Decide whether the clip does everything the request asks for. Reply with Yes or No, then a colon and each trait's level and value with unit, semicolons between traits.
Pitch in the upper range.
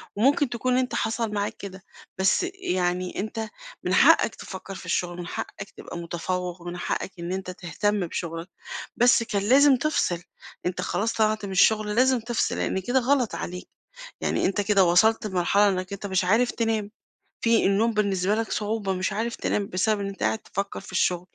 Yes: high, 200 Hz